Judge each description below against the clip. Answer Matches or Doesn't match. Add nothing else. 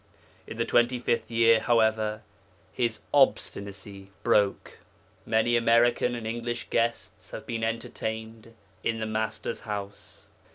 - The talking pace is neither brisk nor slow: Doesn't match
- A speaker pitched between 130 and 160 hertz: Doesn't match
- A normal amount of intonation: Doesn't match